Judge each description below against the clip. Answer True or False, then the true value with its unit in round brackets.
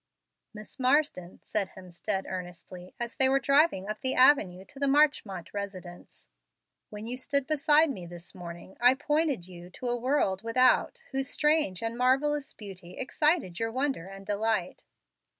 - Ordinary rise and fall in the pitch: False (6.8 semitones)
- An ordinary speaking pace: True (155 wpm)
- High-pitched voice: True (230 Hz)